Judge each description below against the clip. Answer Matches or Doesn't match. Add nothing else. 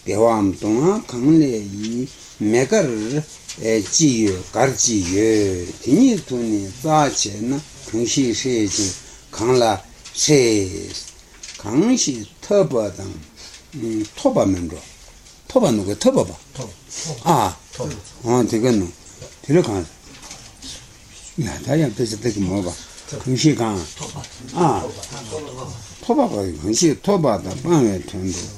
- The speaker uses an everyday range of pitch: Doesn't match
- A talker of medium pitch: Doesn't match